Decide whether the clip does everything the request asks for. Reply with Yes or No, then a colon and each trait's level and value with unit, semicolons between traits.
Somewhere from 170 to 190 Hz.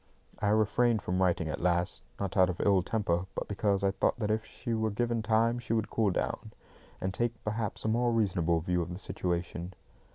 No: low, 100 Hz